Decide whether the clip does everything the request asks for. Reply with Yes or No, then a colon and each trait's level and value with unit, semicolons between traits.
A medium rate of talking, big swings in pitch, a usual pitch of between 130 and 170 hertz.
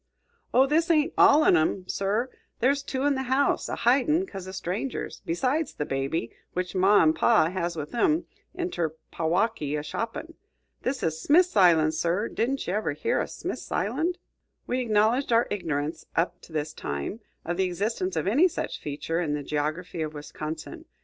No: average, 180 wpm; wide, 8.4 semitones; high, 190 Hz